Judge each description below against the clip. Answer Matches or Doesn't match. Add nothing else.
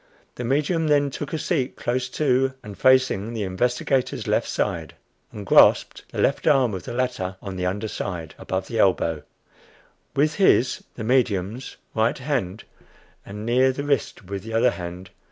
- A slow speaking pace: Doesn't match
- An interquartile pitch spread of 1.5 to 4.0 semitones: Doesn't match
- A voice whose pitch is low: Matches